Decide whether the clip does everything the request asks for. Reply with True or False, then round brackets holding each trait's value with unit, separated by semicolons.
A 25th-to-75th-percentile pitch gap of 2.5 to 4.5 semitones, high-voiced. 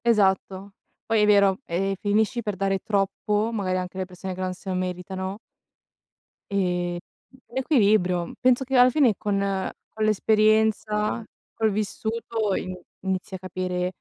True (2.8 semitones; 200 Hz)